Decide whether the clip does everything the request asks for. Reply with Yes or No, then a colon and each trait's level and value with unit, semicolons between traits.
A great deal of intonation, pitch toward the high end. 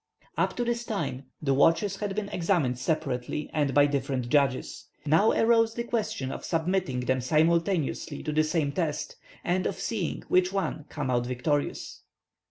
No: wide, 5.9 semitones; medium, 155 Hz